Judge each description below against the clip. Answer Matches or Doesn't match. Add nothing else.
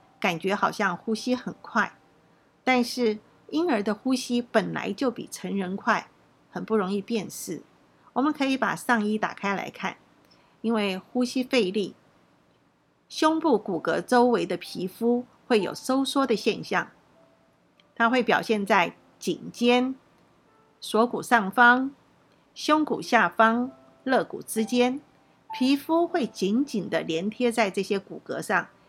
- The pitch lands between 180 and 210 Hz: Doesn't match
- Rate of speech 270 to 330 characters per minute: Doesn't match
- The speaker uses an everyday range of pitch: Matches